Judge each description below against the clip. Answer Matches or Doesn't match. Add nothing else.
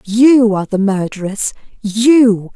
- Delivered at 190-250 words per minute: Doesn't match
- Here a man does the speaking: Doesn't match